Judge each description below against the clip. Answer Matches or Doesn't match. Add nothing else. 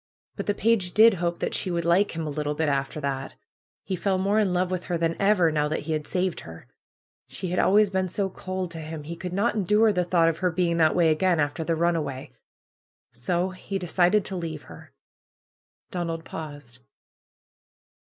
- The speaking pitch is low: Doesn't match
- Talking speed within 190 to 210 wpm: Matches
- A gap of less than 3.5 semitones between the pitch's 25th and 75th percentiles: Matches